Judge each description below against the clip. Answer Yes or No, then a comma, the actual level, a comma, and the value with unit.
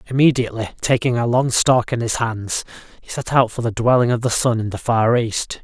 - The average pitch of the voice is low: Yes, low, 120 Hz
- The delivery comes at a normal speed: No, fast, 225 wpm